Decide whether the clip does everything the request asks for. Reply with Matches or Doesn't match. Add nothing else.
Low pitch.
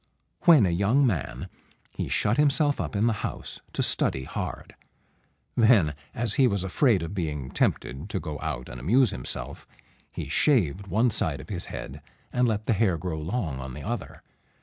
Matches